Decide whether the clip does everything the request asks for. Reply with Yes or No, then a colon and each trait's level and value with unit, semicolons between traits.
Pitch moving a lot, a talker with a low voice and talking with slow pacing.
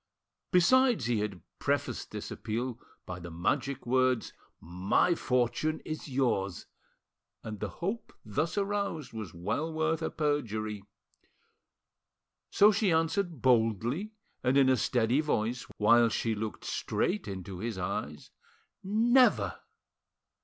Yes: wide, 7.0 semitones; low, 125 Hz; slow, 120 wpm